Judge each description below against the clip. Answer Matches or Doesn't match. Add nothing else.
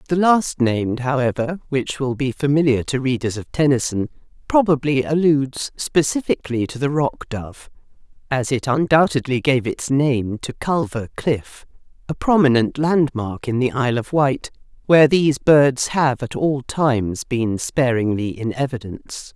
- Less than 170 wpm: Matches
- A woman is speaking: Matches